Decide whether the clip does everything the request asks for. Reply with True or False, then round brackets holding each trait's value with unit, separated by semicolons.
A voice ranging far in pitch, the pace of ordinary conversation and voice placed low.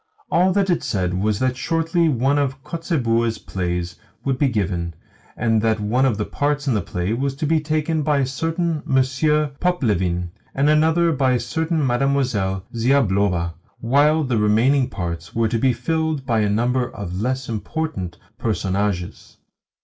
True (6.3 semitones; 165 wpm; 130 Hz)